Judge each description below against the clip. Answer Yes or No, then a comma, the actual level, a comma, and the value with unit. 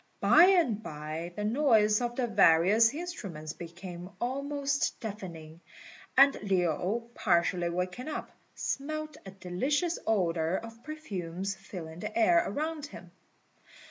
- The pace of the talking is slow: Yes, slow, 120 wpm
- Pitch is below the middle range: No, high, 210 Hz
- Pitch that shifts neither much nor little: No, wide, 8.1 semitones